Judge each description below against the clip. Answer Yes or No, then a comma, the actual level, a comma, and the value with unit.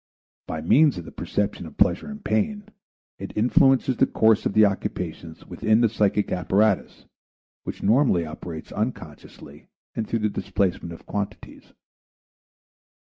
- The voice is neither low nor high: No, low, 105 Hz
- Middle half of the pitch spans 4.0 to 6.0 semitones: Yes, average, 5.2 semitones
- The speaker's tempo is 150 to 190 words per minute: No, slow, 135 wpm